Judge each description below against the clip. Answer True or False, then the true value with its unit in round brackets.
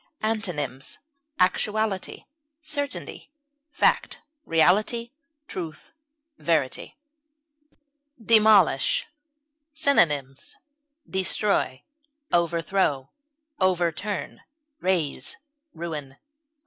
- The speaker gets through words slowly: True (50 wpm)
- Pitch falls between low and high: True (180 Hz)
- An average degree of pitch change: False (5.7 semitones)